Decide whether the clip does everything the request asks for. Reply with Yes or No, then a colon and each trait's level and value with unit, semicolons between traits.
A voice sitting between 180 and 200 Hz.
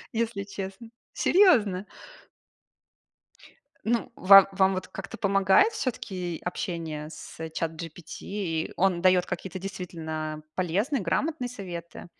Yes: high, 190 Hz